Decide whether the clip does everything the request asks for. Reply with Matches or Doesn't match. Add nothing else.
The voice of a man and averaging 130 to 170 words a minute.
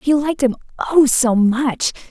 Doesn't match